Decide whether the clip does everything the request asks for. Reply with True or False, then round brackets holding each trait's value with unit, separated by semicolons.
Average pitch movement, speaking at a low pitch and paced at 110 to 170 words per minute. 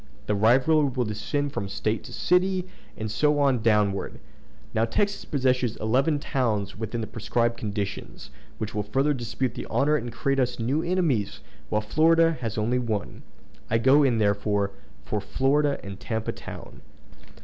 True (5.0 semitones; 120 Hz; 160 wpm)